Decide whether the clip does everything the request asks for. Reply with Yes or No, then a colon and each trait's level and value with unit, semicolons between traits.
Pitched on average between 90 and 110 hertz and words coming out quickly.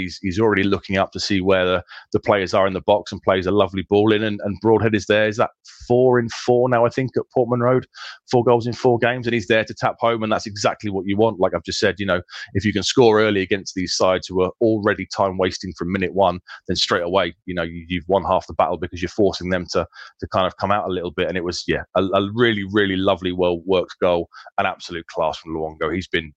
Yes: low, 100 Hz; fast, 270 wpm